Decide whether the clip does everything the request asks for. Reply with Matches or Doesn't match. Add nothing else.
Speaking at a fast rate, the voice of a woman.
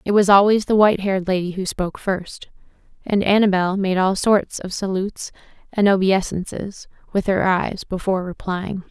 Doesn't match